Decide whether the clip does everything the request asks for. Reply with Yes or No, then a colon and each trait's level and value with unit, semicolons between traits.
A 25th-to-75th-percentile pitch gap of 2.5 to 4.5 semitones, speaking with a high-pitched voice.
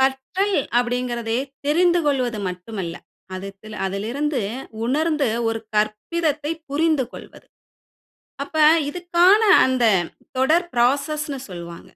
No: wide, 5.6 semitones; very high, 265 Hz